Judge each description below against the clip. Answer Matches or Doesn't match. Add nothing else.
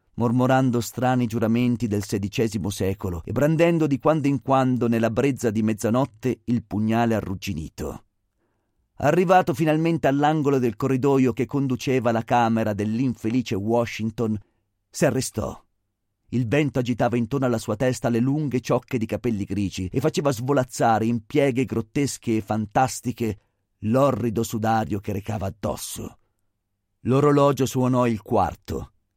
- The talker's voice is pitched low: Matches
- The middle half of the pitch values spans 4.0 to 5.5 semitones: Doesn't match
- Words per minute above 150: Doesn't match